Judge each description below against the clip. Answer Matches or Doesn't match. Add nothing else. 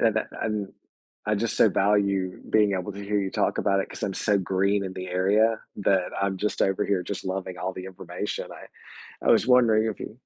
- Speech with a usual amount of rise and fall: Doesn't match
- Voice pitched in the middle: Doesn't match